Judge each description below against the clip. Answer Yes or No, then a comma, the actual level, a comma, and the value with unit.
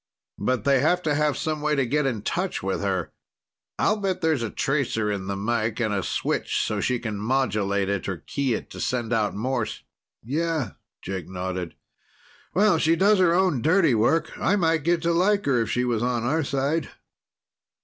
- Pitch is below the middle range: Yes, low, 130 Hz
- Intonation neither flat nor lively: No, wide, 7.1 semitones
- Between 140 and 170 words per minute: No, average, 195 wpm